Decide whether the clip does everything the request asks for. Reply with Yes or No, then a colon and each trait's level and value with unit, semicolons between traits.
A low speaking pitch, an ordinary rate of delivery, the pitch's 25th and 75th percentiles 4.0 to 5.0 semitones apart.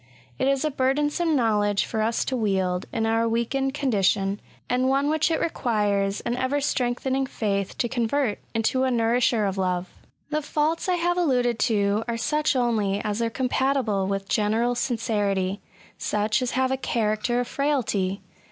No: high, 235 Hz; average, 165 wpm; average, 4.3 semitones